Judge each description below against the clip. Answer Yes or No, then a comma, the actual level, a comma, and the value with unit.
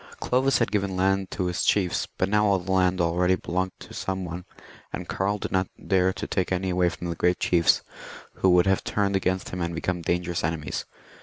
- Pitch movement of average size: No, narrow, 1.5 semitones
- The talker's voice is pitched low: Yes, very low, 95 Hz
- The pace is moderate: No, fast, 215 wpm